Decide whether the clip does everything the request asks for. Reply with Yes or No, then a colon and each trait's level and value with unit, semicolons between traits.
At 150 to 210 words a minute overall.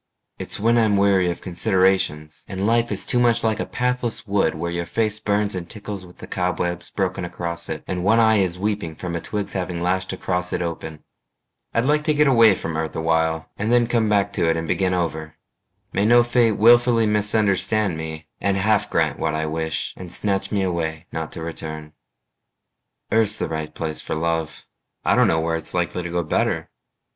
Yes: average, 200 wpm